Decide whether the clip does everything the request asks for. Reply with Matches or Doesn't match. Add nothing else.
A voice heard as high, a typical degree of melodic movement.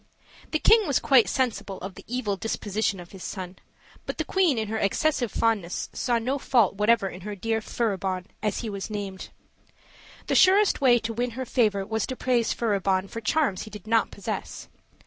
Matches